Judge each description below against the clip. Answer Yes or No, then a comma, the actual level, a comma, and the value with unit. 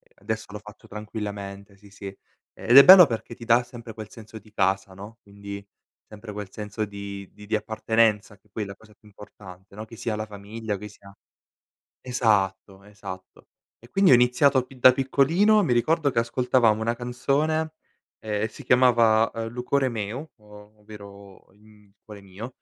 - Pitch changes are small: No, average, 3.2 semitones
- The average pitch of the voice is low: Yes, low, 110 Hz